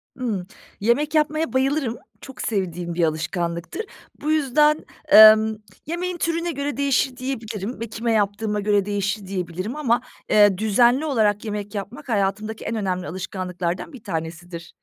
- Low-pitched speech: No, high, 215 Hz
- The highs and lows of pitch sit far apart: Yes, wide, 5.7 semitones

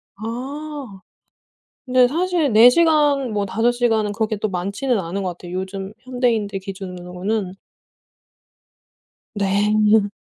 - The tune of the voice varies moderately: Yes, average, 4.4 semitones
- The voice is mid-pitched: No, high, 215 Hz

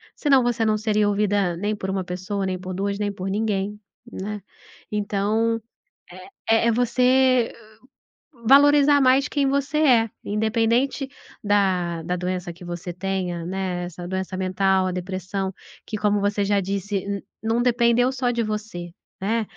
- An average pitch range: Yes, average, 3.6 semitones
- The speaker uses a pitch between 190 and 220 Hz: Yes, high, 205 Hz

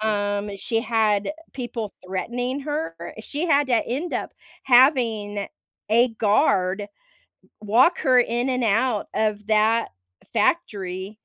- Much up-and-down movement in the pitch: No, average, 3.8 semitones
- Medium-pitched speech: No, high, 225 Hz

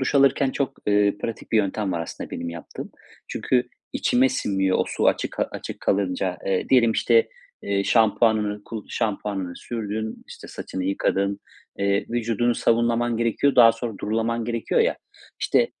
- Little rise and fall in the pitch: No, average, 3.0 semitones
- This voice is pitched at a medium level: No, low, 110 Hz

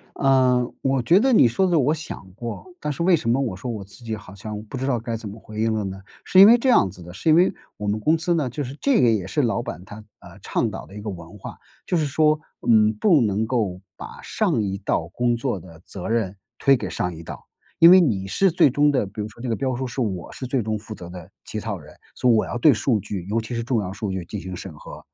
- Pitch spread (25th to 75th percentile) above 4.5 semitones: Yes, average, 5.2 semitones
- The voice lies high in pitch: No, low, 115 Hz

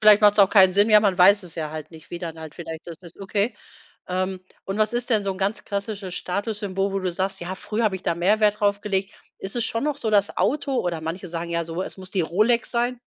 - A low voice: No, high, 195 Hz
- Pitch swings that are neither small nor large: Yes, average, 3.1 semitones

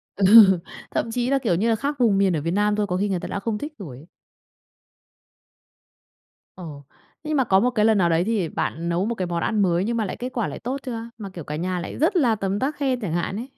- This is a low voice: No, high, 205 Hz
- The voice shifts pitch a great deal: No, average, 4.7 semitones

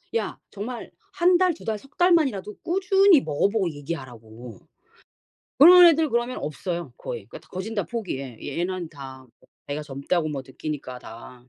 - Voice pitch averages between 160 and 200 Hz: Yes, medium, 185 Hz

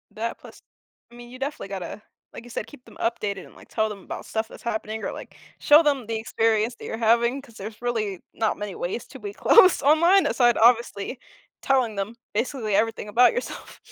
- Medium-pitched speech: No, high, 230 Hz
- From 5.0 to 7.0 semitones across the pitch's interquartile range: No, average, 2.9 semitones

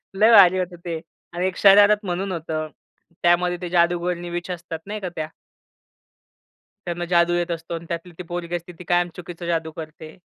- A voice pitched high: No, medium, 175 Hz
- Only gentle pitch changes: Yes, narrow, 1.1 semitones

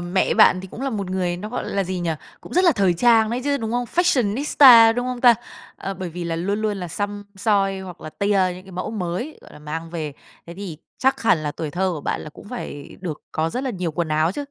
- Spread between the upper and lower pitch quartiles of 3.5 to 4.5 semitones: No, average, 5.0 semitones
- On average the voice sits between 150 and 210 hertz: Yes, high, 195 Hz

